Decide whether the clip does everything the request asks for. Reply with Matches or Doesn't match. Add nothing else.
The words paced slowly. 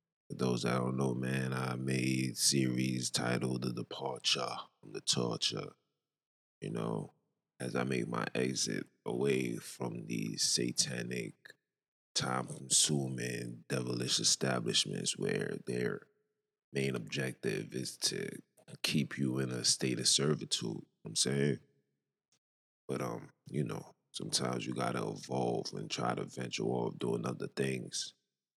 Matches